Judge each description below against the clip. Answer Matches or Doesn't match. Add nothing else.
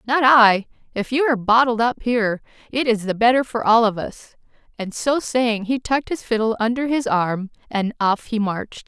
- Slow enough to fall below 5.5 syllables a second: Matches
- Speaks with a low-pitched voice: Doesn't match